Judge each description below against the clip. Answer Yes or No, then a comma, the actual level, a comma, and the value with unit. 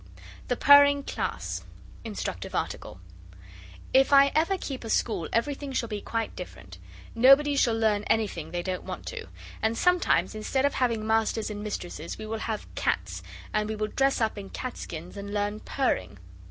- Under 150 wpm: No, average, 170 wpm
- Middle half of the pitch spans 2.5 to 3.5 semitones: No, average, 4.7 semitones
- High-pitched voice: Yes, high, 225 Hz